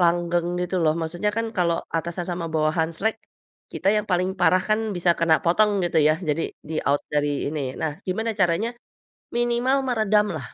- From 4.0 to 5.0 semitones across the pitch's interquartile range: Yes, average, 4.3 semitones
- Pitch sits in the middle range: Yes, medium, 175 Hz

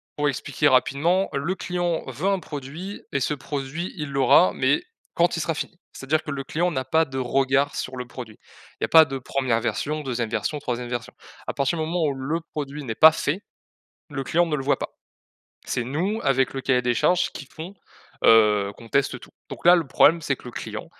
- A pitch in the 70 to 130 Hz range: No, medium, 140 Hz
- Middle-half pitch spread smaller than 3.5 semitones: No, average, 3.8 semitones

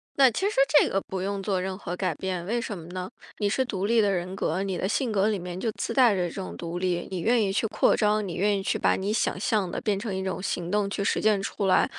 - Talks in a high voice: Yes, high, 195 Hz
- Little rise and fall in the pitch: Yes, narrow, 2.3 semitones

